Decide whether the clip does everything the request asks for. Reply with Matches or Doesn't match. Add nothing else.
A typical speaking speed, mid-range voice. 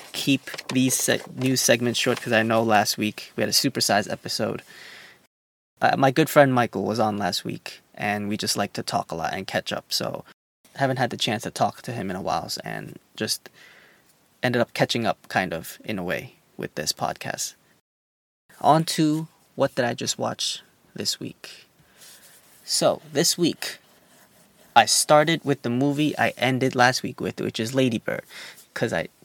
Doesn't match